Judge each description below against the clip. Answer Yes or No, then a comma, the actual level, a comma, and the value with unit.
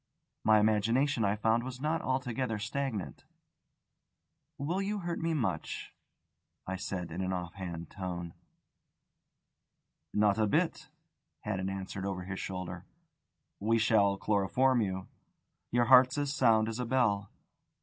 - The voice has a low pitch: Yes, low, 110 Hz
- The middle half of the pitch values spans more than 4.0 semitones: Yes, average, 5.1 semitones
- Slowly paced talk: Yes, slow, 130 wpm